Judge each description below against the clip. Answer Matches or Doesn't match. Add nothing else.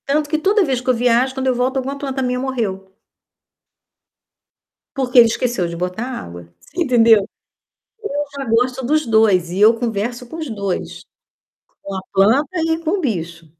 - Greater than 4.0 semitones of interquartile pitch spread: Matches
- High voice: Matches